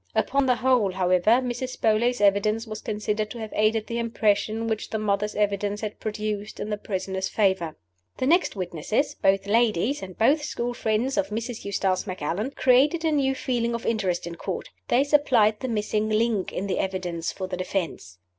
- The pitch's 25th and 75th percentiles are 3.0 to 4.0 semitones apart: Yes, average, 3.4 semitones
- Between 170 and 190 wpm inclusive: Yes, average, 185 wpm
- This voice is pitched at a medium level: No, high, 215 Hz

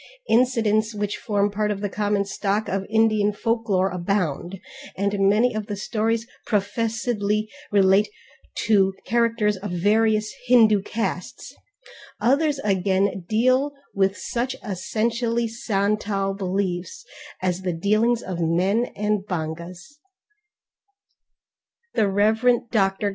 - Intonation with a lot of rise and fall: No, narrow, 2.6 semitones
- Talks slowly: Yes, slow, 110 wpm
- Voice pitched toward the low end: No, high, 210 Hz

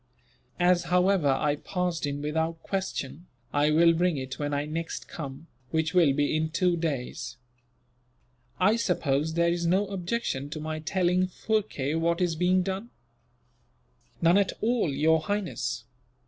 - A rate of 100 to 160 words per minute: Yes, average, 145 wpm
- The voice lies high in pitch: No, medium, 165 Hz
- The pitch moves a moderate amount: Yes, average, 3.6 semitones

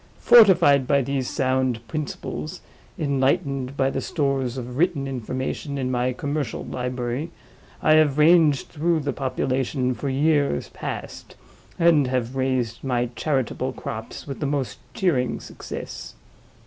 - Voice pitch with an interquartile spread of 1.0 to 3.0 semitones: Yes, narrow, 2.6 semitones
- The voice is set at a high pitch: No, low, 135 Hz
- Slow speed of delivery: Yes, slow, 130 wpm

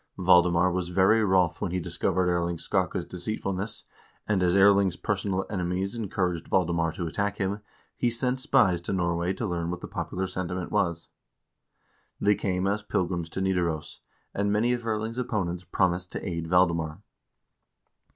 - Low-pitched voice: Yes, very low, 90 Hz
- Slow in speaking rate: No, average, 155 wpm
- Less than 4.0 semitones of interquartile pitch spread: Yes, average, 2.7 semitones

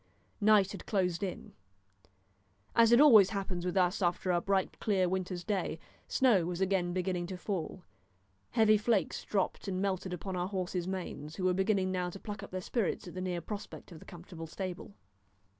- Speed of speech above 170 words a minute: Yes, average, 185 wpm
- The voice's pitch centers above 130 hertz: Yes, medium, 185 Hz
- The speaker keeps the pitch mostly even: Yes, narrow, 2.0 semitones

